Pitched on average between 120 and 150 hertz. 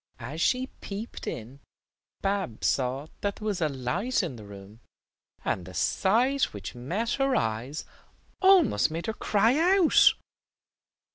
No: medium, 175 Hz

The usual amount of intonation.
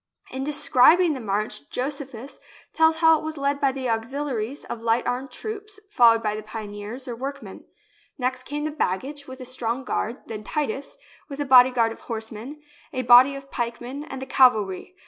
Yes: average, 3.7 semitones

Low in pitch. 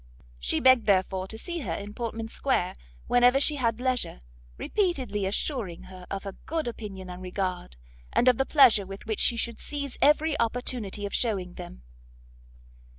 No: high, 225 Hz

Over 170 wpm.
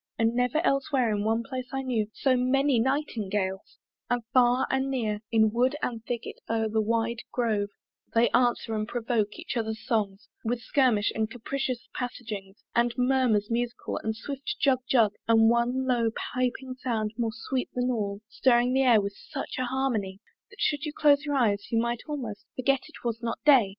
Yes: average, 180 wpm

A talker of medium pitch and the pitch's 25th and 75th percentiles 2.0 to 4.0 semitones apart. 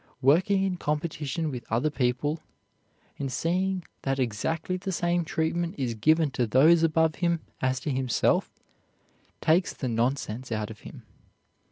No: medium, 150 Hz; average, 4.9 semitones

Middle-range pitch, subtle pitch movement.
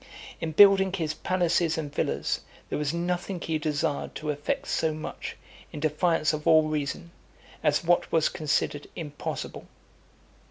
Yes: medium, 160 Hz; narrow, 2.3 semitones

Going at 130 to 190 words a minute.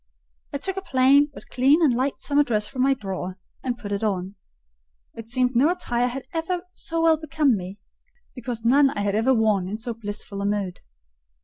No: average, 200 wpm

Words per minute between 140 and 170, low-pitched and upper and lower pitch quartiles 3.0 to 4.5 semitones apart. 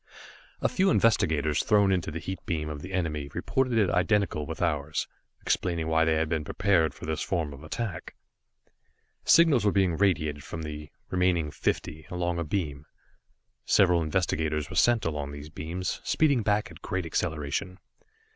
Yes: average, 165 wpm; very low, 85 Hz; average, 3.8 semitones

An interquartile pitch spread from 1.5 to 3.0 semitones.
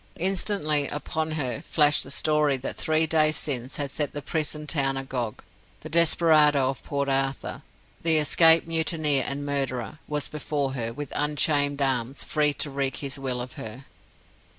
Yes: narrow, 2.4 semitones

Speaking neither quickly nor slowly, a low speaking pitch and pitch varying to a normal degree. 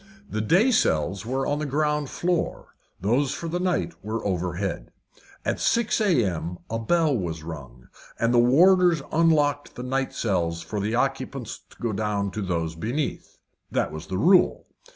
No: average, 165 wpm; low, 120 Hz; wide, 8.0 semitones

